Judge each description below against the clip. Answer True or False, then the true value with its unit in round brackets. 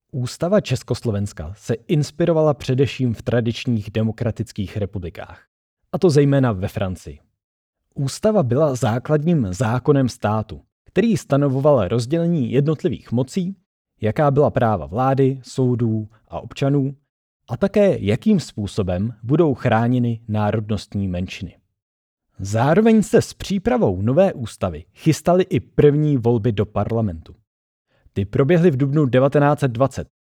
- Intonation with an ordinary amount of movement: False (5.8 semitones)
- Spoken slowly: True (110 wpm)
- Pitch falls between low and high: False (125 Hz)